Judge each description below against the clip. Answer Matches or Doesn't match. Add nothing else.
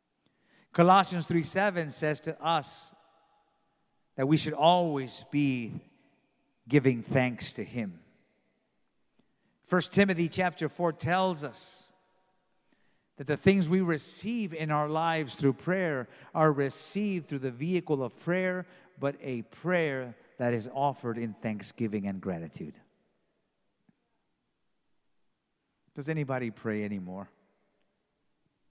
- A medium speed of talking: Doesn't match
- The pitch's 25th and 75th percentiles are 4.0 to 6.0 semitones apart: Matches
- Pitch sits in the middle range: Matches